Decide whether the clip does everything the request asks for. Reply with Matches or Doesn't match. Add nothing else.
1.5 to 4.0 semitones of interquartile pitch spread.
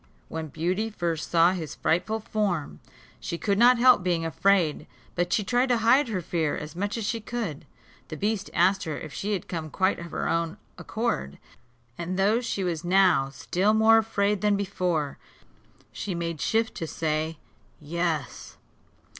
Doesn't match